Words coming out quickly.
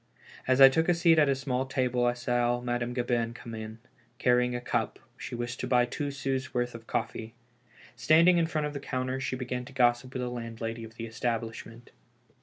Yes: fast, 210 wpm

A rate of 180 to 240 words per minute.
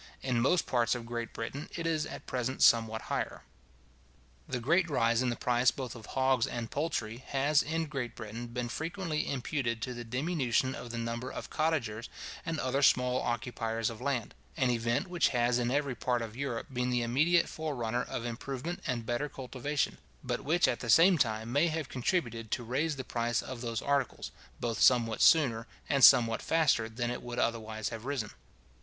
Yes: average, 185 wpm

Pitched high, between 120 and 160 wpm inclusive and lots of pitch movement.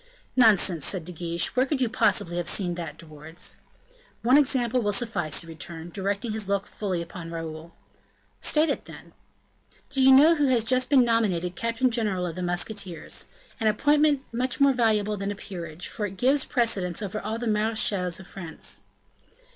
No: high, 205 Hz; average, 180 wpm; wide, 5.7 semitones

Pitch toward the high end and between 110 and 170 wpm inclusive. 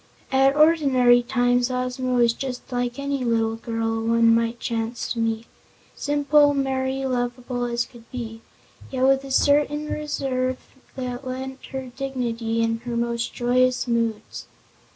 Yes: very high, 250 Hz; average, 140 wpm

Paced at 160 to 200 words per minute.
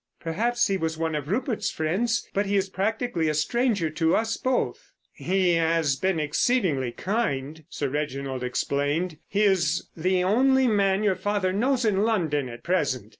Yes: average, 165 wpm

